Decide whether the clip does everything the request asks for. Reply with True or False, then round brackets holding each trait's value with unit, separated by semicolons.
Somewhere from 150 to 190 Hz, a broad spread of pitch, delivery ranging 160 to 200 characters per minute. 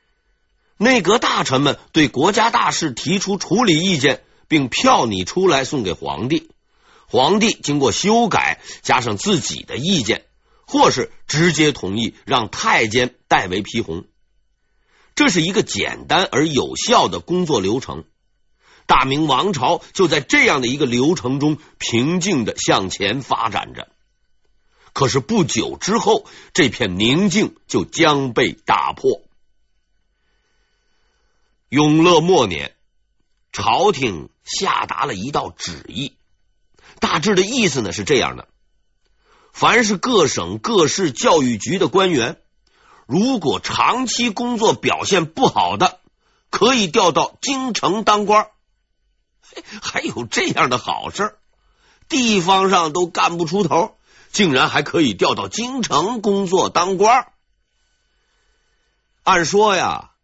True (185 Hz; 6.4 semitones; 185 characters per minute)